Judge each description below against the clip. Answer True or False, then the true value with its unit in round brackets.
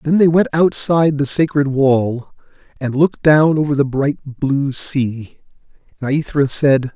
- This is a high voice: False (140 Hz)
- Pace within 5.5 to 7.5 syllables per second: False (4.2 syllables/s)